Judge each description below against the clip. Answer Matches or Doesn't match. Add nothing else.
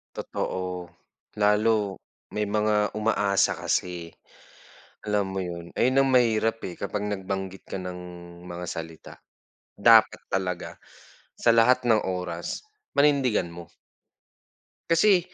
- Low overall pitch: Matches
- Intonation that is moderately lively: Matches